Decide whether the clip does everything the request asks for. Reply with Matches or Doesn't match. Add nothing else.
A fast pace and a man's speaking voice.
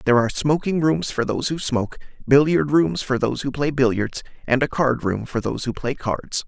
Matches